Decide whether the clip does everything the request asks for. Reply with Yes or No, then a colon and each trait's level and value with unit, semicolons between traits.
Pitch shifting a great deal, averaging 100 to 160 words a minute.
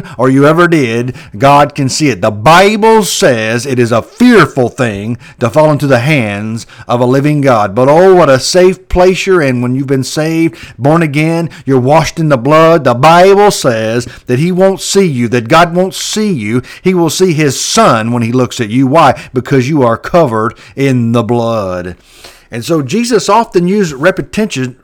No: wide, 5.9 semitones; average, 195 wpm